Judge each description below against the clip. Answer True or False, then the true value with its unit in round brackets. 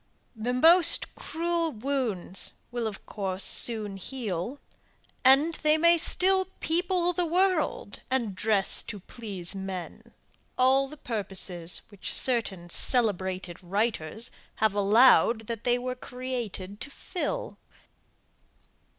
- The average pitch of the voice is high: True (235 Hz)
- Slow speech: True (115 wpm)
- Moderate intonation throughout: False (6.3 semitones)